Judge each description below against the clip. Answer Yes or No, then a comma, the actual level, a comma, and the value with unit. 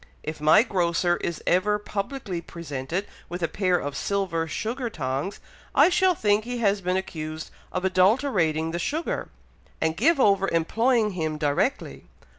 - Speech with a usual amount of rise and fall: Yes, average, 4.7 semitones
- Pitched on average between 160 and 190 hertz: Yes, medium, 185 Hz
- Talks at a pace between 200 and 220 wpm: No, average, 150 wpm